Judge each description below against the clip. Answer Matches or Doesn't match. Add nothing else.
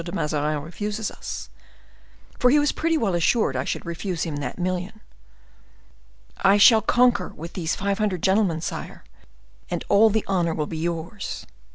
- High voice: Doesn't match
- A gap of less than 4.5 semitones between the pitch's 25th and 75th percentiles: Doesn't match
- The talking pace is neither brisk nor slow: Matches